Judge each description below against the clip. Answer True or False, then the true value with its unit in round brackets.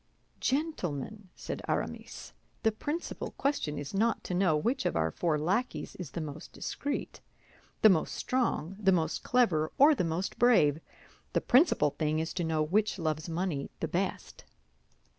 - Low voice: False (180 Hz)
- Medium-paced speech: True (160 wpm)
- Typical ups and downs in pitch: False (7.0 semitones)